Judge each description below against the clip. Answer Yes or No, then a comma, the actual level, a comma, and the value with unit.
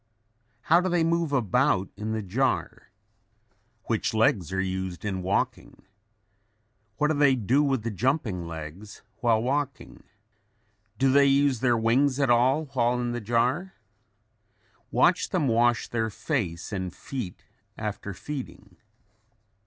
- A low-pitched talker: Yes, low, 120 Hz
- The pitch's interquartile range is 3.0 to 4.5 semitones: No, average, 5.1 semitones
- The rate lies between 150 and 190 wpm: No, slow, 135 wpm